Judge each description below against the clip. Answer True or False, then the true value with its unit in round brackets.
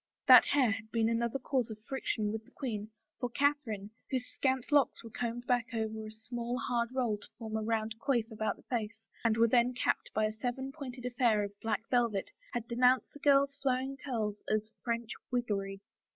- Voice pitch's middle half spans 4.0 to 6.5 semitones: False (2.6 semitones)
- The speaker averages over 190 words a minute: True (200 wpm)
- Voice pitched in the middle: False (235 Hz)